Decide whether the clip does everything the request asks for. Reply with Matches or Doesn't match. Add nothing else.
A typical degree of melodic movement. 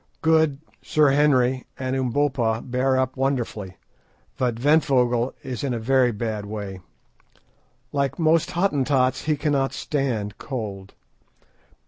Matches